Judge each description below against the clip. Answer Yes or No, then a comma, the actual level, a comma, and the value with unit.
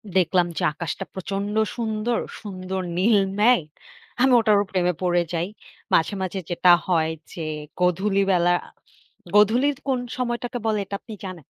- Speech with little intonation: No, average, 3.6 semitones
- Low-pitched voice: No, high, 195 Hz